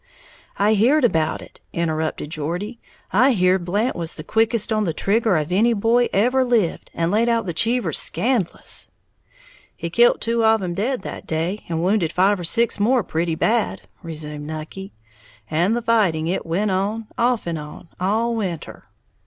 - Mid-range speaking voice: No, high, 200 Hz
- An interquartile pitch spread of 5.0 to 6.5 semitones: Yes, wide, 5.4 semitones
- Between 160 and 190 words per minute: Yes, average, 170 wpm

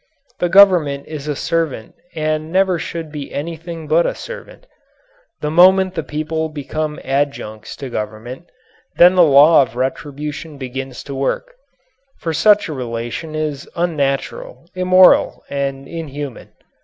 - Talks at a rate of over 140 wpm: No, slow, 135 wpm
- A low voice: No, medium, 155 Hz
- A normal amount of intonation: Yes, average, 3.6 semitones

